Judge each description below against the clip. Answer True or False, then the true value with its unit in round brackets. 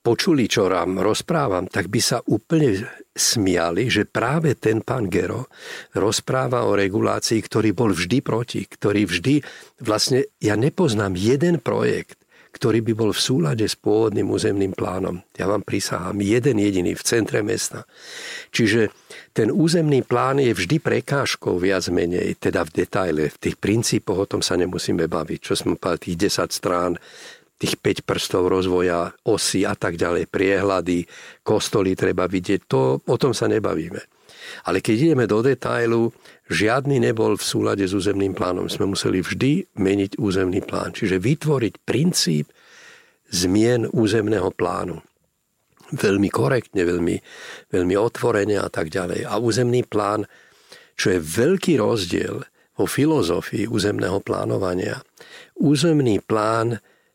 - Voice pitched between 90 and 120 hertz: True (110 Hz)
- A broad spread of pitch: True (6.1 semitones)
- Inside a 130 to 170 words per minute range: True (140 wpm)